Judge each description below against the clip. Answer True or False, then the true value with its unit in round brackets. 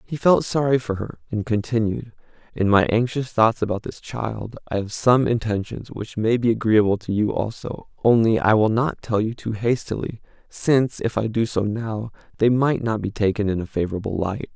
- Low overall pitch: True (110 Hz)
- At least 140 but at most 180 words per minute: False (200 wpm)